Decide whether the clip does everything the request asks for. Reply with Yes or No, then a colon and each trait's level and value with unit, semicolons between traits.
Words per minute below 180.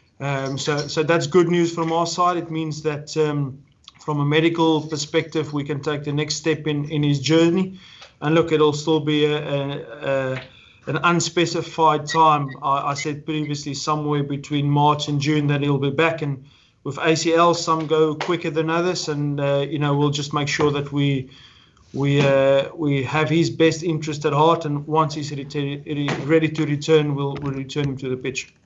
No: average, 195 wpm